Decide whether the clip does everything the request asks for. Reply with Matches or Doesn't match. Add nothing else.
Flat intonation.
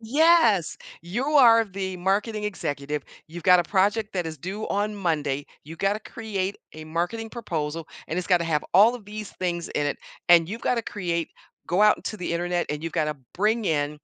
Doesn't match